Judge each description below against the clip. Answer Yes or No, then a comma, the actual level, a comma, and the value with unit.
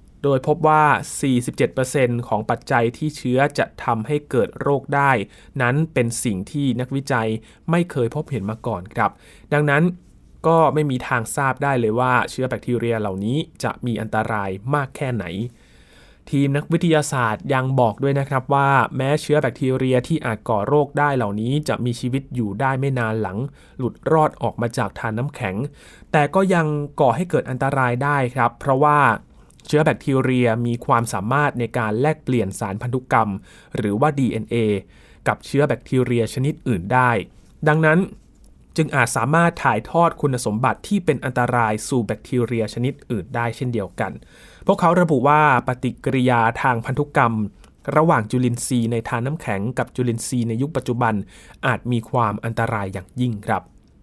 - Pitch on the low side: Yes, low, 125 Hz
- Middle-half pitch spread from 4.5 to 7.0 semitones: No, average, 3.9 semitones